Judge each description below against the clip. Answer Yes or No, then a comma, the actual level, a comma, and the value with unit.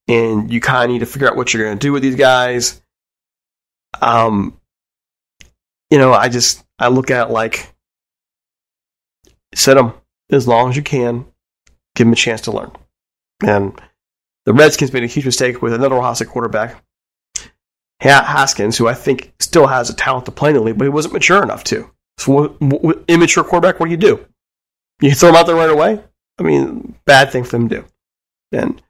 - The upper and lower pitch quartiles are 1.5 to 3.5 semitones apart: No, average, 4.1 semitones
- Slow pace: No, average, 195 wpm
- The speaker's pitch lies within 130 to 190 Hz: No, low, 120 Hz